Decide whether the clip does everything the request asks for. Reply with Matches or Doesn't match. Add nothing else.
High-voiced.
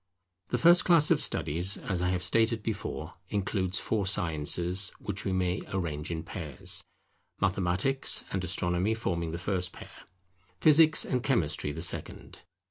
Doesn't match